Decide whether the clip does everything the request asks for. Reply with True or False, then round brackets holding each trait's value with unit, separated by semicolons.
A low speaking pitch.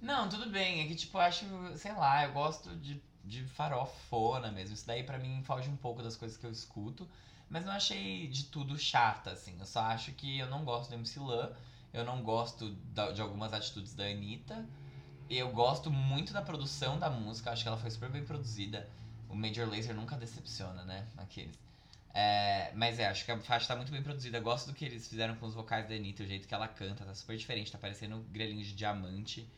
True (115 Hz)